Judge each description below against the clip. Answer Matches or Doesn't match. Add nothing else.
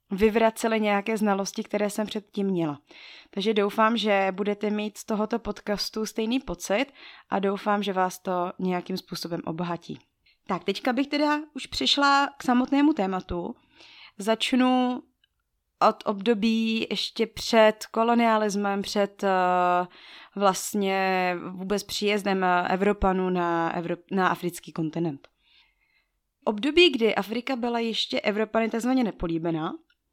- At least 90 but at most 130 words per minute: Matches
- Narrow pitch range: Doesn't match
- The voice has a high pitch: Matches